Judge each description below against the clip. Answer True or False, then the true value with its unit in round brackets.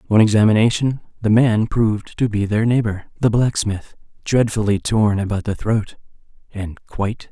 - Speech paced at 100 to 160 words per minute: True (155 wpm)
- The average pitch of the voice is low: True (110 Hz)